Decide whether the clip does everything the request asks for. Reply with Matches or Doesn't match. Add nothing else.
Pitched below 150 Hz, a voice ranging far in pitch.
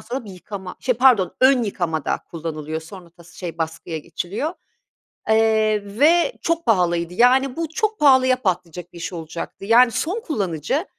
Doesn't match